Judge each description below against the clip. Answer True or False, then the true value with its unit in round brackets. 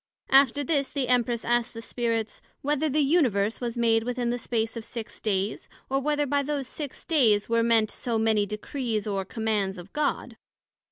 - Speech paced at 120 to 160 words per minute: False (180 wpm)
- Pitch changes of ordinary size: True (3.7 semitones)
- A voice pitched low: False (235 Hz)